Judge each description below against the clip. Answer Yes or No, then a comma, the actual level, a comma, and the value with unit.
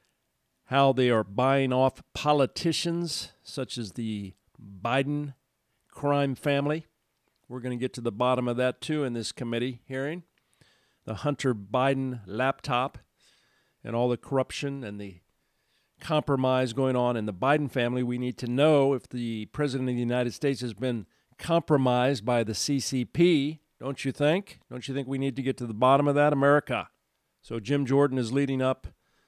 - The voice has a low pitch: Yes, low, 130 Hz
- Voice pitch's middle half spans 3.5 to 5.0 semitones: No, narrow, 2.6 semitones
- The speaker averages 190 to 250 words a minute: No, average, 170 wpm